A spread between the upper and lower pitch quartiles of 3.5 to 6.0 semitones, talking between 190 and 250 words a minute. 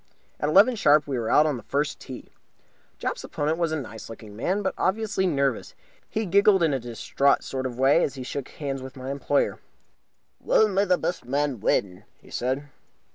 Yes: average, 4.9 semitones; average, 200 wpm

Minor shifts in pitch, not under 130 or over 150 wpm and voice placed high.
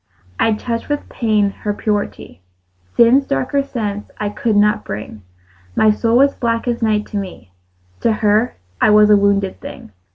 No: narrow, 2.2 semitones; average, 165 wpm; high, 210 Hz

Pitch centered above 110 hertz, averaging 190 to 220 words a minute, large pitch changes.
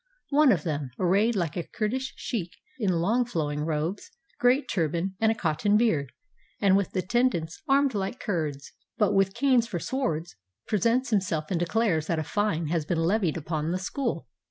No: high, 190 Hz; average, 180 wpm; wide, 5.8 semitones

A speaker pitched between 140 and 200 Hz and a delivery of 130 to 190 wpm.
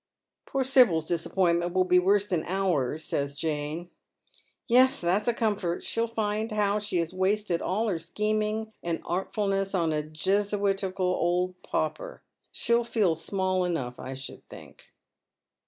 Yes: medium, 185 Hz; average, 150 wpm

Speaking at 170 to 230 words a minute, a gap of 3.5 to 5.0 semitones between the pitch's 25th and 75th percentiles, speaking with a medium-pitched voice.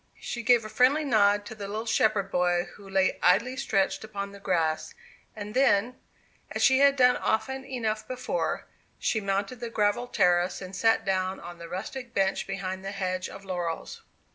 No: average, 180 wpm; average, 4.0 semitones; high, 205 Hz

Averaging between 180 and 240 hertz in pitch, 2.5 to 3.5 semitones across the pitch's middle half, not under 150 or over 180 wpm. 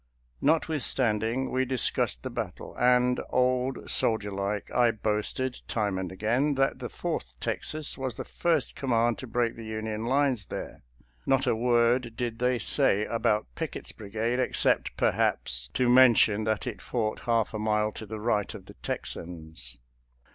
No: low, 115 Hz; average, 3.0 semitones; average, 160 wpm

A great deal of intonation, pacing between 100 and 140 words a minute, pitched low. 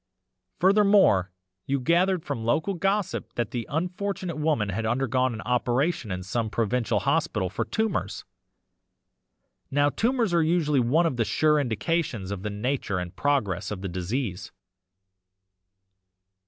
Yes: wide, 7.9 semitones; slow, 135 wpm; low, 130 Hz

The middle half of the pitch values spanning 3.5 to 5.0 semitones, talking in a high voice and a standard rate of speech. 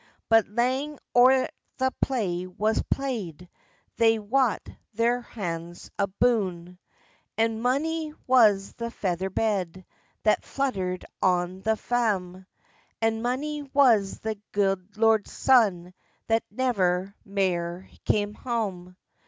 No: average, 4.7 semitones; high, 215 Hz; slow, 110 wpm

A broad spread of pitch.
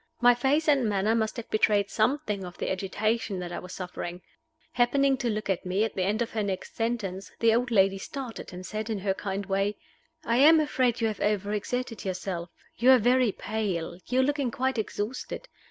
No: average, 4.0 semitones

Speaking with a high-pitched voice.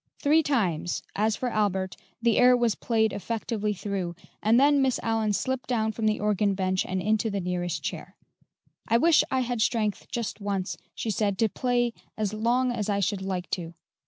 Yes: high, 215 Hz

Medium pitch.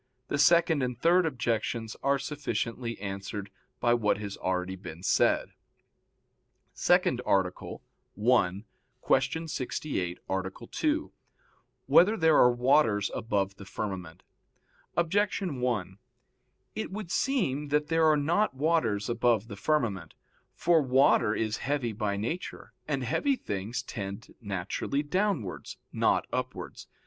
No: low, 120 Hz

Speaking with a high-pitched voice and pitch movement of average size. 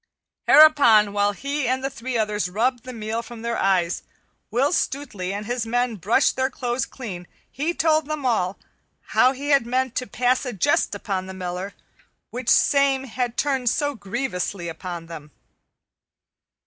Yes: high, 235 Hz; average, 4.7 semitones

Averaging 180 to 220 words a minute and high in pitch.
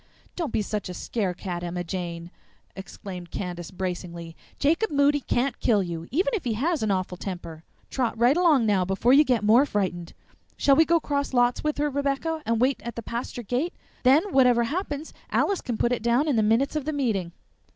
Yes: fast, 205 wpm; high, 235 Hz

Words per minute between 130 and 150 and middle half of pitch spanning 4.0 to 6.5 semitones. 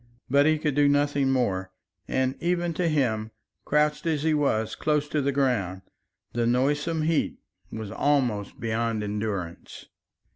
Yes: average, 145 wpm; average, 5.2 semitones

